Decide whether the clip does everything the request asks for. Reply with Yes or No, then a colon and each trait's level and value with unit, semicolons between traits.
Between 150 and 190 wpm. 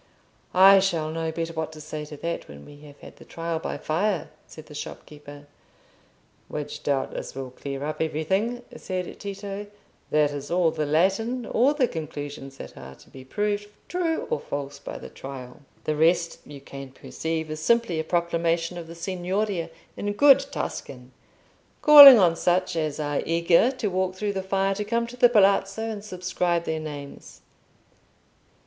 Yes: average, 170 wpm